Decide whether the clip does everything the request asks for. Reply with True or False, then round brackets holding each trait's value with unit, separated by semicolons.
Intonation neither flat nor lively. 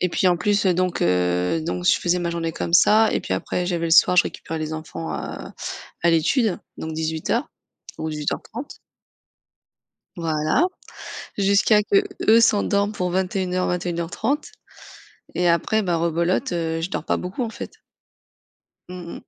True (3.6 semitones)